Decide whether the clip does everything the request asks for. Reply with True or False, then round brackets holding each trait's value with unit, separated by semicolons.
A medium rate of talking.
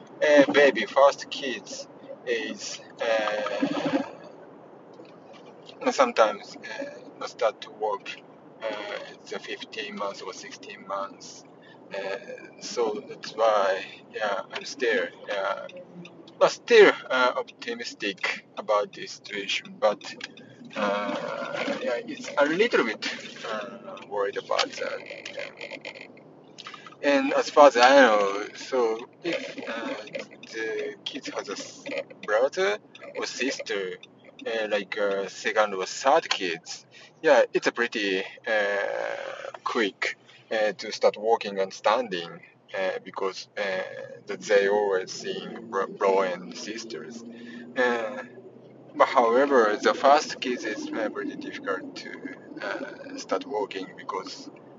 False (115 wpm)